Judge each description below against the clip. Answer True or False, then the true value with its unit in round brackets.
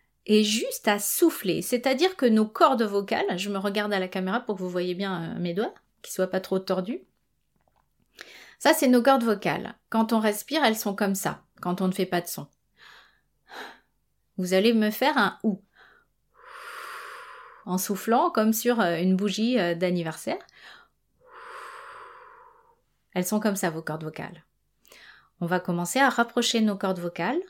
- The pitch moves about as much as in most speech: True (4.4 semitones)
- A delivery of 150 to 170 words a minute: True (160 wpm)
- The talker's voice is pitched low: False (210 Hz)